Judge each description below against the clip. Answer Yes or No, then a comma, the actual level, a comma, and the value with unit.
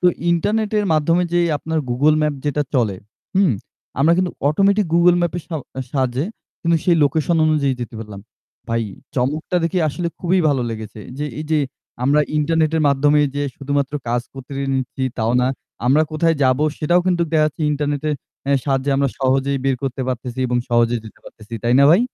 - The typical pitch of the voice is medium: Yes, medium, 145 Hz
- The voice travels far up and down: No, average, 4.0 semitones